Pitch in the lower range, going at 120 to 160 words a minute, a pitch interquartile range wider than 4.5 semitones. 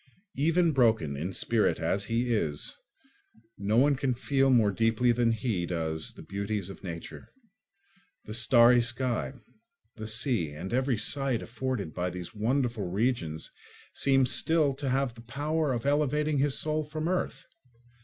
Yes: low, 120 Hz; average, 150 wpm; average, 5.1 semitones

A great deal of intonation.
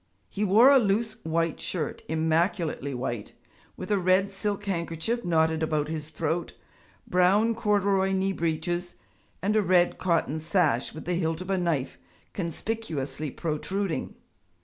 No: average, 3.7 semitones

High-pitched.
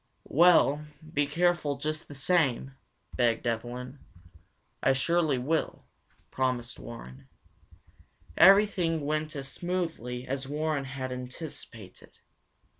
No: medium, 140 Hz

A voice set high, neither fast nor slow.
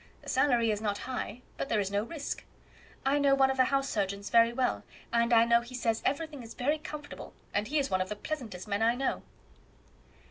No: high, 240 Hz; fast, 220 wpm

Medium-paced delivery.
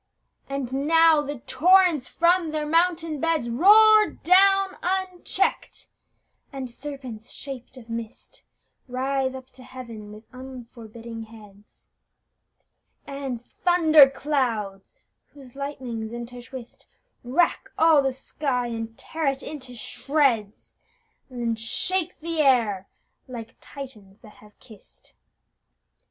No: slow, 110 wpm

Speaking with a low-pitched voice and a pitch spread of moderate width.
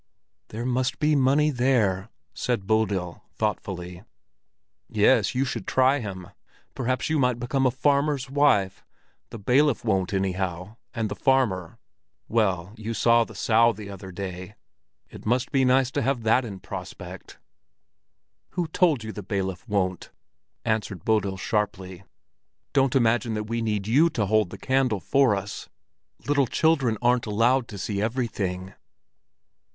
Yes: low, 115 Hz; average, 4.8 semitones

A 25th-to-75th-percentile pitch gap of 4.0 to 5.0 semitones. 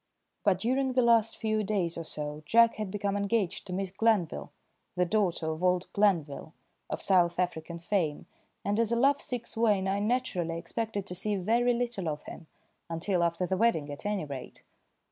Yes: average, 4.7 semitones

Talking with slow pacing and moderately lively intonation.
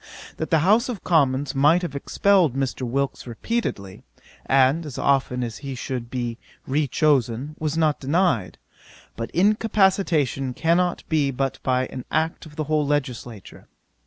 No: average, 150 wpm; average, 4.2 semitones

